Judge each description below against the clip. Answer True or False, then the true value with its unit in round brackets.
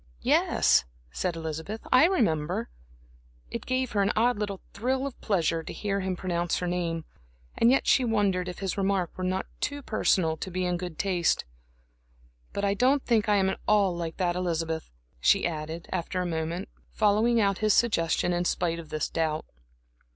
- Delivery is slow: False (180 wpm)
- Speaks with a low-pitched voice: False (185 Hz)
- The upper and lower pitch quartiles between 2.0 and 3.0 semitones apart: False (3.9 semitones)